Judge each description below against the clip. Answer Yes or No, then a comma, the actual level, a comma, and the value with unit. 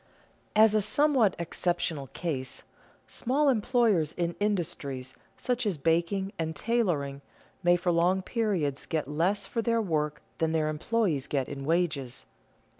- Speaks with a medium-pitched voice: Yes, medium, 175 Hz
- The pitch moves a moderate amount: No, wide, 5.9 semitones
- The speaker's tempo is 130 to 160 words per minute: Yes, average, 140 wpm